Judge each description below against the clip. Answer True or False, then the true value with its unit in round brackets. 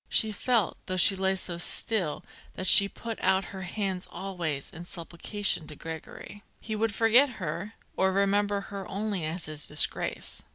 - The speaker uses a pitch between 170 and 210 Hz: True (190 Hz)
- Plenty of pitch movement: False (3.1 semitones)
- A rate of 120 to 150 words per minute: False (165 wpm)